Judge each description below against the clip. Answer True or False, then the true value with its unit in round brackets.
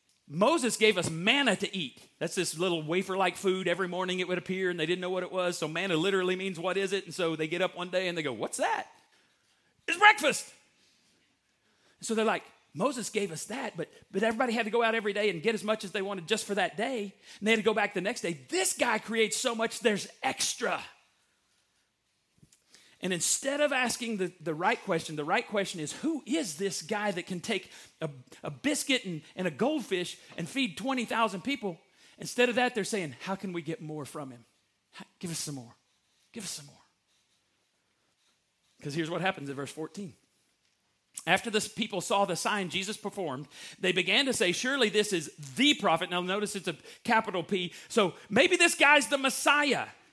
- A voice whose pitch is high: True (195 Hz)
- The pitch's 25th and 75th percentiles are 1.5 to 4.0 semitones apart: False (4.5 semitones)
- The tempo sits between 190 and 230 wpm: True (205 wpm)